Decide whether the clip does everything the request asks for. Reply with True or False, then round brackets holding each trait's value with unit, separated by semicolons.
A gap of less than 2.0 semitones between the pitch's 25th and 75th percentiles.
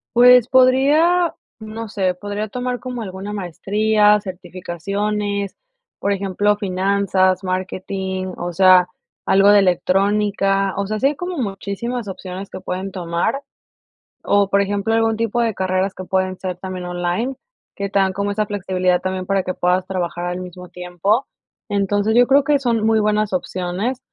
False (2.6 semitones)